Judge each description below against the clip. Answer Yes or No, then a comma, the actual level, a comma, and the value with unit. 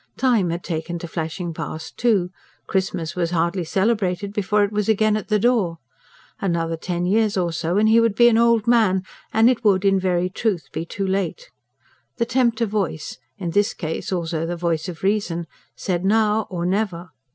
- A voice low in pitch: No, high, 190 Hz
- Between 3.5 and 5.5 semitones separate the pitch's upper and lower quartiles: Yes, average, 4.0 semitones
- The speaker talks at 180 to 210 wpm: Yes, average, 185 wpm